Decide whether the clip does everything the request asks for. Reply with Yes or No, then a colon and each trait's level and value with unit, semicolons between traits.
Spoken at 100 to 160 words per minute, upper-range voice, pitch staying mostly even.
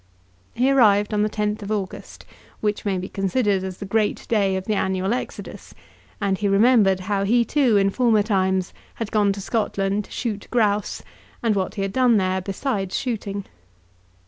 No: average, 180 wpm; high, 205 Hz; narrow, 2.3 semitones